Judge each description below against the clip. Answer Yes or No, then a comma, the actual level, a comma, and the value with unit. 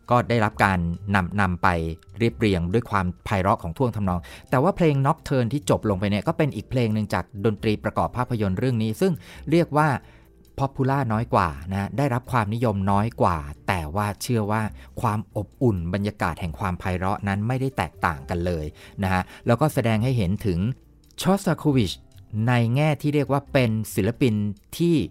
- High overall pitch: No, low, 110 Hz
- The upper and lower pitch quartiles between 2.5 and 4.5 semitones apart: No, average, 5.1 semitones